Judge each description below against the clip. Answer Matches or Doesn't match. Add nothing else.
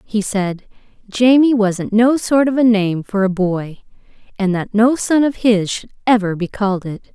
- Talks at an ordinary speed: Matches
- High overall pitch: Matches